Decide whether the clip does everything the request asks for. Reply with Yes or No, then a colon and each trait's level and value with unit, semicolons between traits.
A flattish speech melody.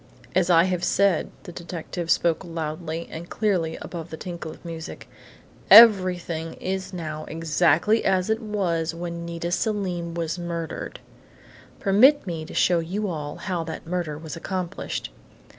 Yes: narrow, 2.2 semitones